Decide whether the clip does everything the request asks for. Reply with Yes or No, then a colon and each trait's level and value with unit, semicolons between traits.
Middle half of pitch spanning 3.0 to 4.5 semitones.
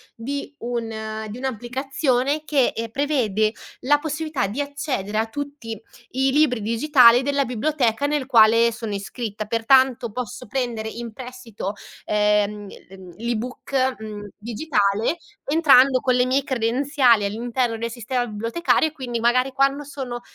Yes: average, 3.6 semitones